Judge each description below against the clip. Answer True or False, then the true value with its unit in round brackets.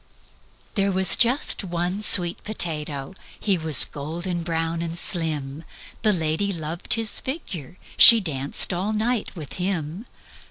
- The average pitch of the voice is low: False (175 Hz)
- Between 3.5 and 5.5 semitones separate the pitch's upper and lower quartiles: True (4.0 semitones)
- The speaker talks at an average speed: False (130 wpm)